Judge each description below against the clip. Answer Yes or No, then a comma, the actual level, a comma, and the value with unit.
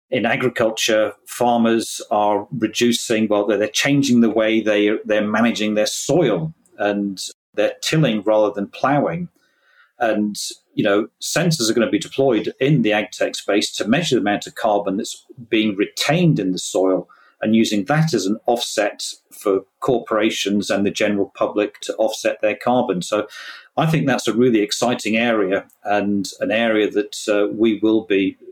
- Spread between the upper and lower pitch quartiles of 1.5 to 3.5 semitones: Yes, narrow, 2.5 semitones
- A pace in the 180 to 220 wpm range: No, average, 165 wpm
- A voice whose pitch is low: Yes, low, 110 Hz